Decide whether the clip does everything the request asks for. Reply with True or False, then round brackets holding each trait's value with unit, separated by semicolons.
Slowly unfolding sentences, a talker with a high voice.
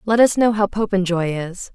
False (205 wpm; 195 Hz)